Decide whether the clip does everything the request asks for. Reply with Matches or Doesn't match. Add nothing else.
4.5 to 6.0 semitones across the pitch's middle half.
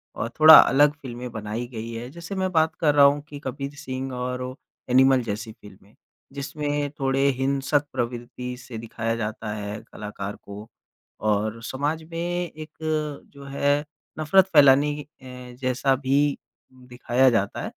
Doesn't match